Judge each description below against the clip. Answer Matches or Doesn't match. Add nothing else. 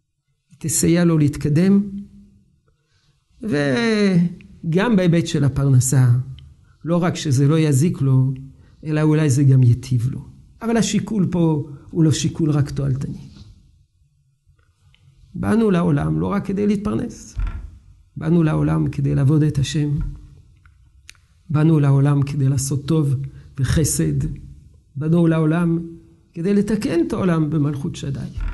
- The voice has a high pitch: Doesn't match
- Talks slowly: Doesn't match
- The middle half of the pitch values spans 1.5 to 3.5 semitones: Doesn't match